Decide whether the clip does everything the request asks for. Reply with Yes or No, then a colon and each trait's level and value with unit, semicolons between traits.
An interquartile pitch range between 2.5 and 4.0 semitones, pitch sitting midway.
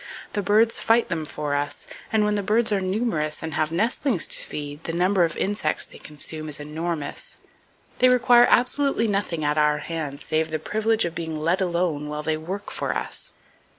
No: wide, 5.5 semitones; medium, 170 Hz